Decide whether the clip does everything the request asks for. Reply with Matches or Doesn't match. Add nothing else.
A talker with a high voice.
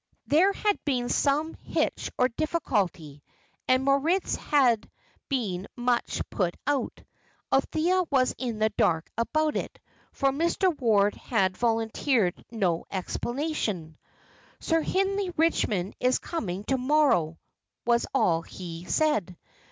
Matches